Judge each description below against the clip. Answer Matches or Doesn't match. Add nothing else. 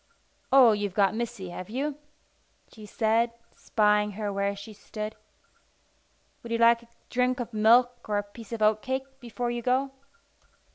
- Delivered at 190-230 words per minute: Doesn't match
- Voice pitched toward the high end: Matches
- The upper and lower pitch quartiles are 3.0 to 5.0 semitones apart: Doesn't match